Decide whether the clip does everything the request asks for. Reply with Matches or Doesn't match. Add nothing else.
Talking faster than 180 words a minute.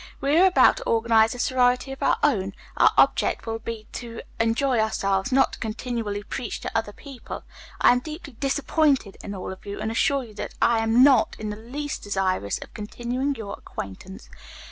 Matches